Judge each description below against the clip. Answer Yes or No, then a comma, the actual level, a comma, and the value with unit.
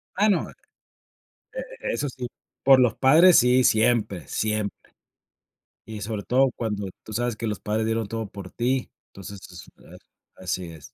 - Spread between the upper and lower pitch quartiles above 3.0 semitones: Yes, average, 3.9 semitones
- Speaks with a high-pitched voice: No, low, 115 Hz